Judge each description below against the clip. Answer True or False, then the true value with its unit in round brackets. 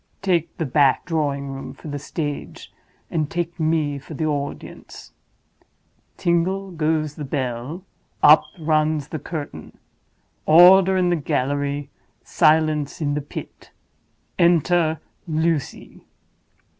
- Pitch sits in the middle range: True (155 Hz)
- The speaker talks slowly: True (110 wpm)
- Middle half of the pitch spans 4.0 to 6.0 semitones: False (2.7 semitones)